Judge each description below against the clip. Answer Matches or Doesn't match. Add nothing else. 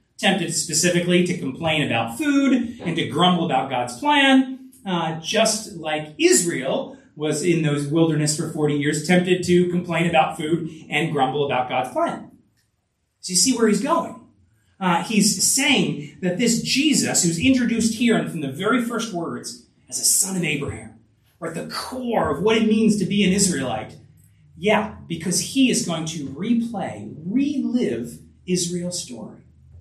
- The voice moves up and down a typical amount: Doesn't match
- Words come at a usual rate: Matches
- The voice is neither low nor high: Matches